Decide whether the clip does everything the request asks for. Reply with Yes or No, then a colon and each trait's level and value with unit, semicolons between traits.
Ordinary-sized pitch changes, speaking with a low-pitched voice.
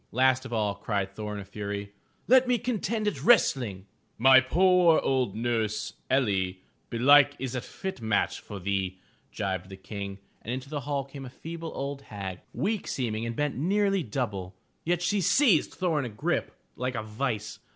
No: wide, 7.1 semitones; low, 125 Hz